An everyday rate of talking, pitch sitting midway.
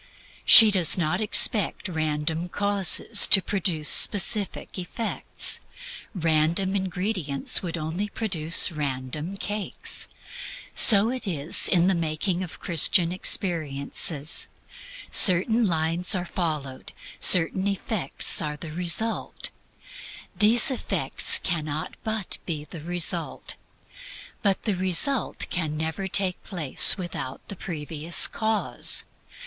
No: slow, 110 wpm; medium, 175 Hz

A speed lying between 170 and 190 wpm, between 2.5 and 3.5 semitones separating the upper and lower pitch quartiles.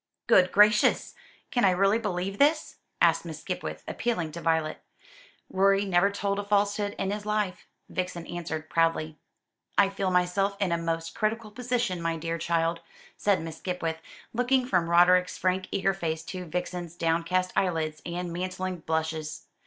No: average, 155 wpm; average, 3.2 semitones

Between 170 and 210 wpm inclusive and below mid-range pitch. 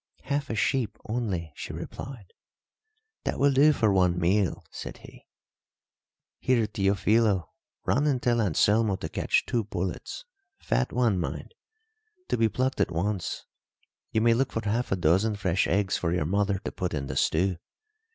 No: average, 160 wpm; low, 105 Hz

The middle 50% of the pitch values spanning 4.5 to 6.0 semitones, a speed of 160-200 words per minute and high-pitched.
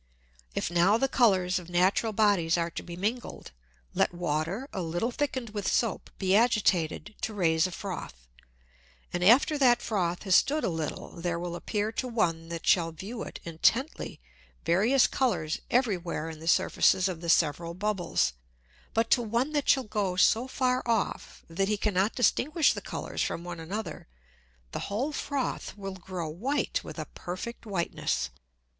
Yes: wide, 5.4 semitones; average, 170 wpm; high, 195 Hz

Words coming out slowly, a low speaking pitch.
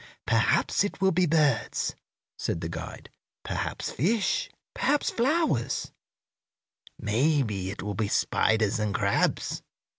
Yes: slow, 115 wpm; low, 120 Hz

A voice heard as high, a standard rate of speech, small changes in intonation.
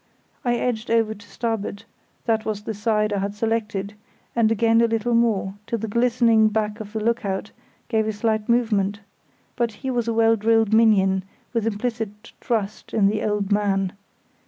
Yes: high, 220 Hz; average, 170 wpm; narrow, 1.8 semitones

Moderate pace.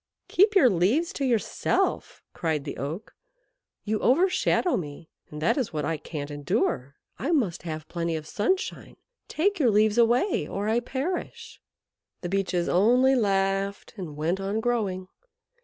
Yes: average, 150 wpm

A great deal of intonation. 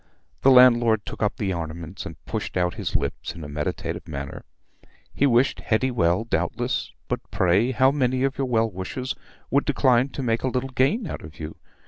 Yes: wide, 6.7 semitones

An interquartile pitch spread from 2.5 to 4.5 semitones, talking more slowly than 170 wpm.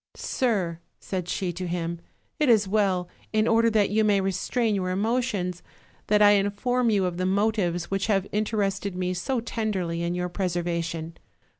No: average, 3.3 semitones; average, 175 wpm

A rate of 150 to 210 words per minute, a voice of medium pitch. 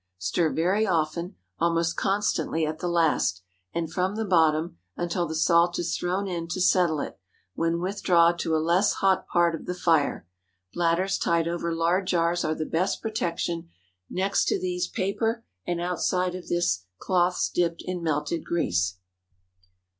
Yes: average, 155 wpm; medium, 170 Hz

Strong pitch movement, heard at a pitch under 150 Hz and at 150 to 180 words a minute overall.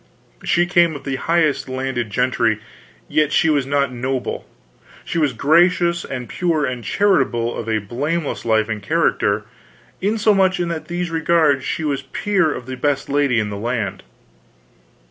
Yes: wide, 5.7 semitones; medium, 140 Hz; average, 160 wpm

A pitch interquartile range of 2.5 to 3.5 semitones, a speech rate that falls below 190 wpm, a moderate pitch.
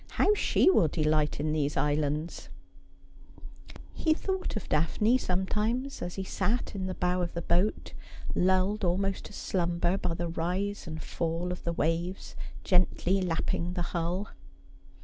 Yes: average, 2.9 semitones; average, 150 wpm; medium, 180 Hz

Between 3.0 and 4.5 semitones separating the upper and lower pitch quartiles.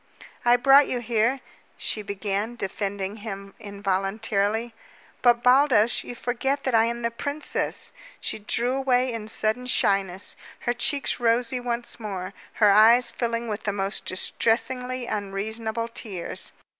Yes: average, 3.3 semitones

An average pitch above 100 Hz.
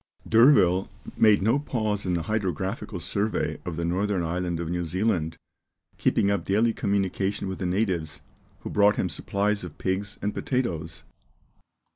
No: very low, 95 Hz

